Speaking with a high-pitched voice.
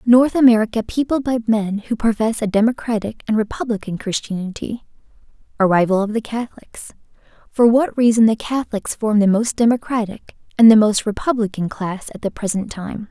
Yes: high, 220 Hz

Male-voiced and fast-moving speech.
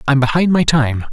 Yes: male; fast, 270 wpm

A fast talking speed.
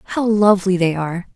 No: average, 180 wpm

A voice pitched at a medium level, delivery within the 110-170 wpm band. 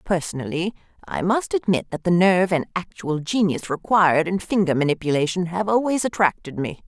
Yes: medium, 180 Hz; average, 155 wpm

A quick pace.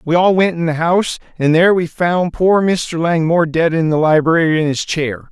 Yes: fast, 225 wpm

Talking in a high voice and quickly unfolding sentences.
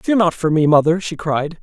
No: medium, 165 Hz; fast, 260 wpm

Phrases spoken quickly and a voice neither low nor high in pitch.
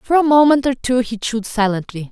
No: fast, 225 wpm; high, 240 Hz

